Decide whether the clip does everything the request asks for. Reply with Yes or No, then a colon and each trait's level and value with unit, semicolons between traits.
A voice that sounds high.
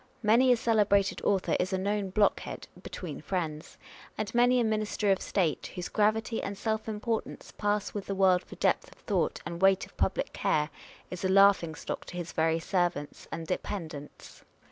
Yes: high, 195 Hz